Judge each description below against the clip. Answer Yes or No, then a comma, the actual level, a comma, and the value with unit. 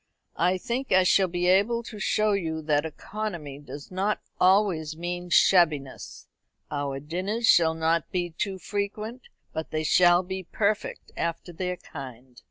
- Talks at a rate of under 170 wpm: Yes, average, 150 wpm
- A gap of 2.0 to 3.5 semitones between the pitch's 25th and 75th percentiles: No, average, 3.9 semitones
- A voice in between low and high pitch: Yes, medium, 175 Hz